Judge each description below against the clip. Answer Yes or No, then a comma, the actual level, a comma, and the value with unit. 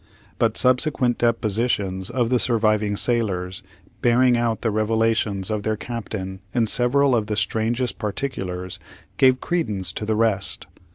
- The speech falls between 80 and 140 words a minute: Yes, slow, 135 wpm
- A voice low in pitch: Yes, low, 110 Hz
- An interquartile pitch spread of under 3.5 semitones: Yes, average, 2.9 semitones